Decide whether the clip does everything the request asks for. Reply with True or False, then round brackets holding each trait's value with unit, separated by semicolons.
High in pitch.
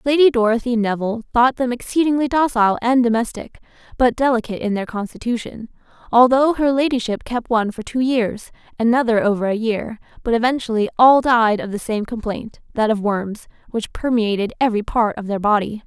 True (230 Hz)